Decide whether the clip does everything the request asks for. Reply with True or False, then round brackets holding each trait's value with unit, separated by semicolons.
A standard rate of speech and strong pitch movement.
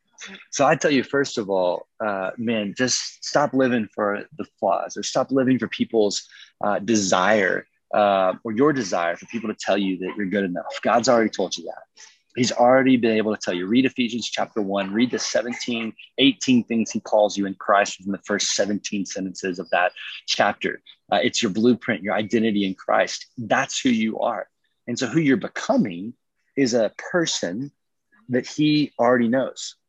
False (185 wpm; 4.1 semitones)